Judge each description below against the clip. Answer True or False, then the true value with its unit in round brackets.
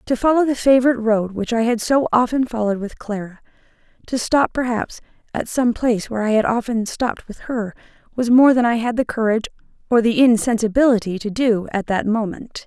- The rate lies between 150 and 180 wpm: False (195 wpm)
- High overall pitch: True (230 Hz)